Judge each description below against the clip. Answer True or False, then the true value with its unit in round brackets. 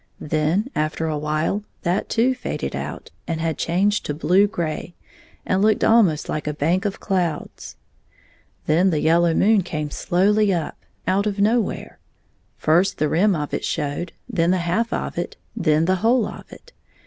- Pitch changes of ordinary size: True (4.5 semitones)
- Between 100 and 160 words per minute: False (170 wpm)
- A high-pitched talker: False (175 Hz)